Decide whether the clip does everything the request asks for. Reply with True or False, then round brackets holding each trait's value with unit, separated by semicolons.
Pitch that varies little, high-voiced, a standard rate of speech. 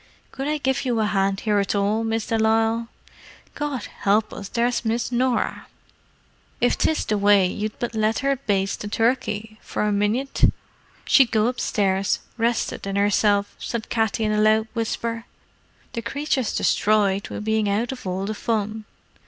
True (2.3 semitones; 220 Hz; 170 wpm)